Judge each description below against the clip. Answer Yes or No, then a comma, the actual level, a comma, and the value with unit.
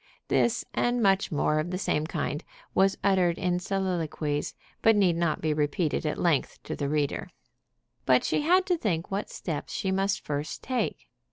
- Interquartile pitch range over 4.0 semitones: Yes, average, 4.4 semitones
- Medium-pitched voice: Yes, medium, 175 Hz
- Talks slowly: No, average, 175 wpm